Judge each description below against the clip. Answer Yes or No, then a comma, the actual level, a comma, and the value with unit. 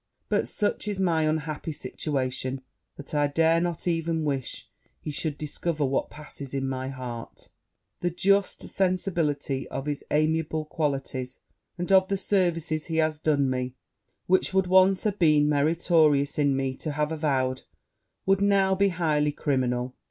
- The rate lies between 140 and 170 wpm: Yes, average, 150 wpm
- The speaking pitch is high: No, medium, 155 Hz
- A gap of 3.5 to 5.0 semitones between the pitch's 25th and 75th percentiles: Yes, average, 3.9 semitones